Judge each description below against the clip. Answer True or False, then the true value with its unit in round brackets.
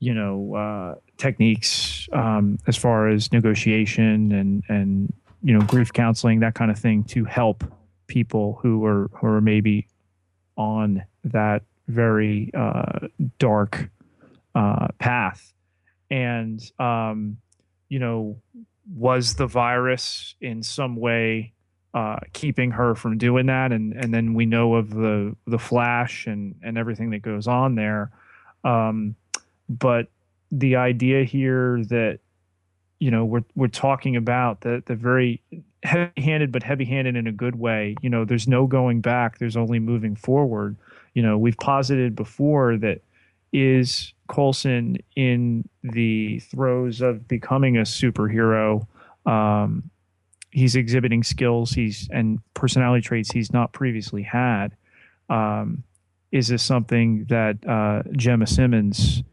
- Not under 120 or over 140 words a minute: True (135 wpm)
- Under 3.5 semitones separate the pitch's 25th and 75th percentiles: True (2.7 semitones)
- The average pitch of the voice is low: True (115 Hz)